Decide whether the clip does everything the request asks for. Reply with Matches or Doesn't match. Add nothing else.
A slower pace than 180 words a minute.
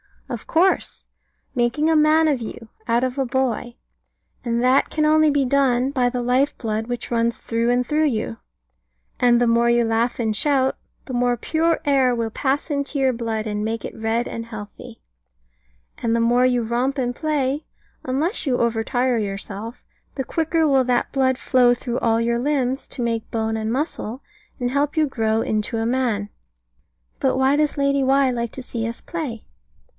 Doesn't match